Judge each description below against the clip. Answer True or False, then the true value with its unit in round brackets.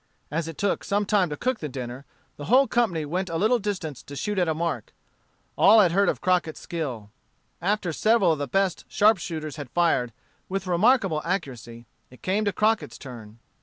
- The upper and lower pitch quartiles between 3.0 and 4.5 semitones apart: False (5.6 semitones)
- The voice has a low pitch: False (175 Hz)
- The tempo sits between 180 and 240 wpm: True (195 wpm)